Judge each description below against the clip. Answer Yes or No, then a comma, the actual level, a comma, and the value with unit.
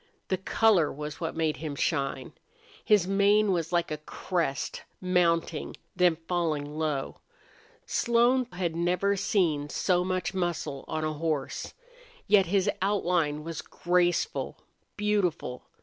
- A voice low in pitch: No, medium, 175 Hz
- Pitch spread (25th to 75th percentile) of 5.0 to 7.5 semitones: No, average, 3.5 semitones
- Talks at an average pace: No, slow, 125 wpm